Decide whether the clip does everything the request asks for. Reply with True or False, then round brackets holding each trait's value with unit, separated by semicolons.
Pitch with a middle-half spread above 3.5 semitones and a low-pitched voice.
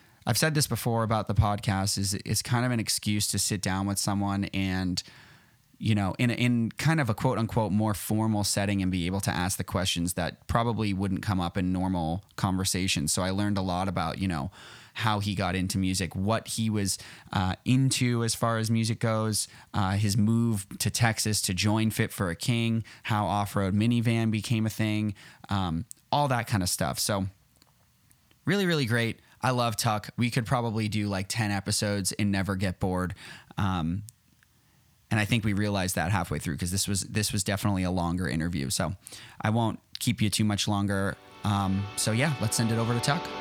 False (3.0 semitones; 105 Hz)